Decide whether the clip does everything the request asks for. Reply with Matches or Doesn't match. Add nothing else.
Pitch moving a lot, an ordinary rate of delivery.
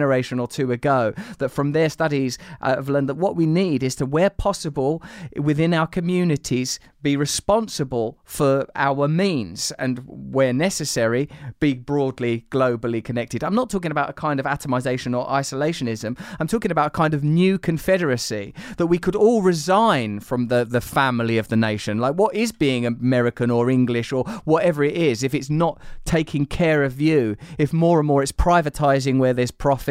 Doesn't match